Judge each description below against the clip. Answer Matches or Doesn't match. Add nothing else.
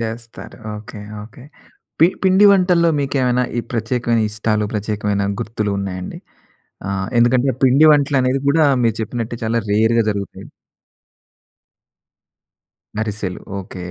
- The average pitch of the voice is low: Matches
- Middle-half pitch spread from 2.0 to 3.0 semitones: Doesn't match